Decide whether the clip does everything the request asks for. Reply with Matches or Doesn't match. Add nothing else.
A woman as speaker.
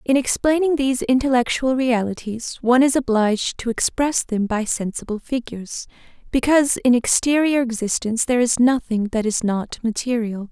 Matches